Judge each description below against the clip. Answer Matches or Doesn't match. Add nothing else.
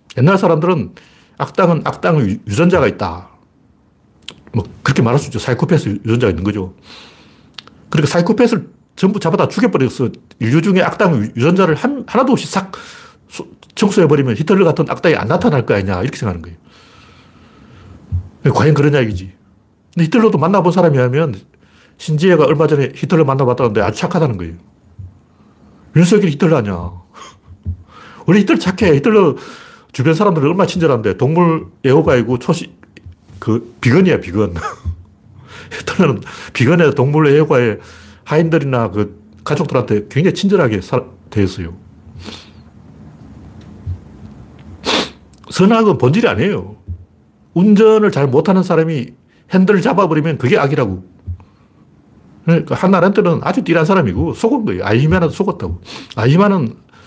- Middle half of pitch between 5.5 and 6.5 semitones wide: Doesn't match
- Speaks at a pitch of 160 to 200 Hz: Doesn't match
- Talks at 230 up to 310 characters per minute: Doesn't match